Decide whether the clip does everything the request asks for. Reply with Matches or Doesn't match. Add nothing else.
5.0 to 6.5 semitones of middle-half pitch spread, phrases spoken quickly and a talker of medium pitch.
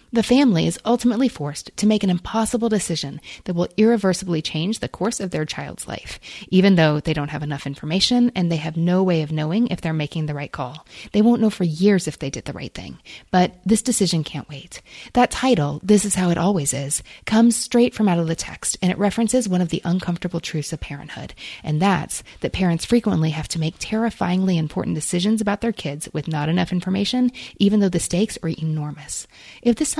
Matches